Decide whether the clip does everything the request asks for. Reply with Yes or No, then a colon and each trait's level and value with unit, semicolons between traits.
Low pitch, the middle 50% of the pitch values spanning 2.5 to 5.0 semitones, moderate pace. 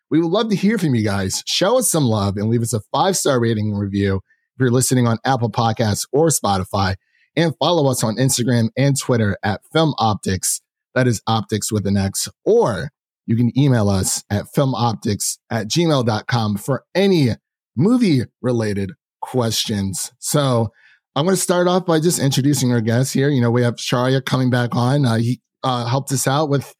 Yes: low, 125 Hz; average, 4.3 semitones; average, 190 wpm